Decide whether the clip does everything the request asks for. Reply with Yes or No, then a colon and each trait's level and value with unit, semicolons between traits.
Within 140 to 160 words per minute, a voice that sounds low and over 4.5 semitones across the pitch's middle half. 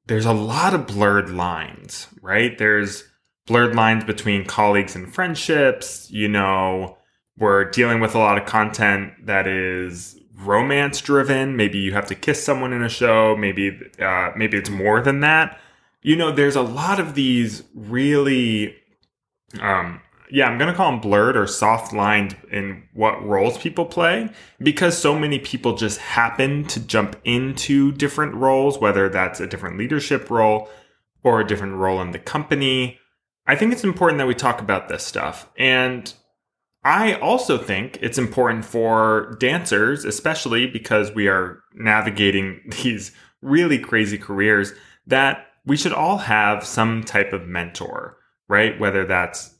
Yes: average, 155 wpm; low, 110 Hz; average, 5.2 semitones